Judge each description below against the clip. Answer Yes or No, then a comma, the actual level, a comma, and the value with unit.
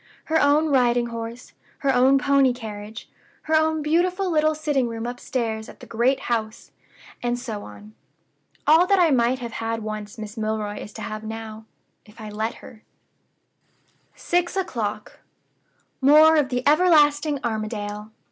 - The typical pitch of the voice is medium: No, high, 245 Hz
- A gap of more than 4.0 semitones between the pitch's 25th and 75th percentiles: Yes, average, 5.2 semitones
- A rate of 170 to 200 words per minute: No, average, 150 wpm